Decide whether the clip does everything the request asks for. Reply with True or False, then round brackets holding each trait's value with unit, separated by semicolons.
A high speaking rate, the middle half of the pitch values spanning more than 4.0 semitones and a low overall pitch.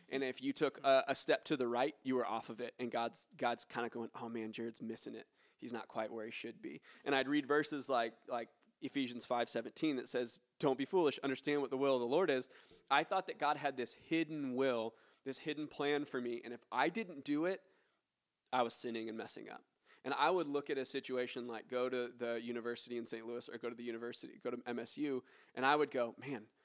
False (245 wpm; 3.3 semitones; 125 Hz)